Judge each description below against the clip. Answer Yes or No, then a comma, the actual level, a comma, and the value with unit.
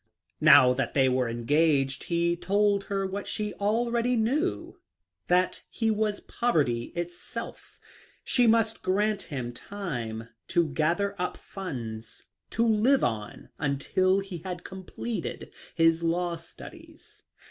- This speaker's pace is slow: Yes, slow, 125 wpm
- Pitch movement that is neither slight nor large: No, wide, 6.9 semitones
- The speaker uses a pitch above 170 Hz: Yes, medium, 185 Hz